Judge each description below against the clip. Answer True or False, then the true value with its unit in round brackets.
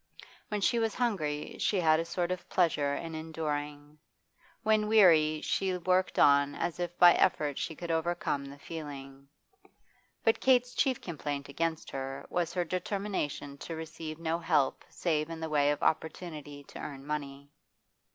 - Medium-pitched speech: True (160 Hz)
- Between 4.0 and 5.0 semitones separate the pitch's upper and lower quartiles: False (3.4 semitones)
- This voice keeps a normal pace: True (160 wpm)